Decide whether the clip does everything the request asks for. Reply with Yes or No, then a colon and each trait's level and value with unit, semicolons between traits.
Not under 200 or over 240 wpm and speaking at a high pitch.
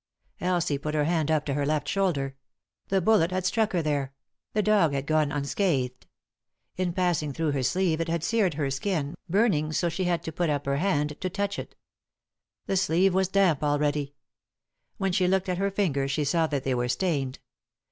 No: fast, 205 wpm; medium, 160 Hz